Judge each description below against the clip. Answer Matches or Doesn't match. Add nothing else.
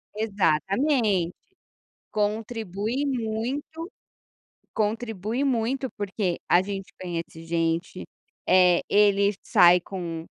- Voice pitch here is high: Matches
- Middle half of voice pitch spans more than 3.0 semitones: Matches